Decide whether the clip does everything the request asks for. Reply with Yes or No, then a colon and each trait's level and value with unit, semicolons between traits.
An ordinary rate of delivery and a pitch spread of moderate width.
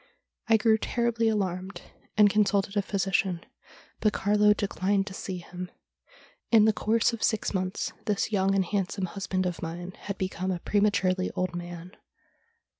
No: average, 155 wpm; narrow, 2.2 semitones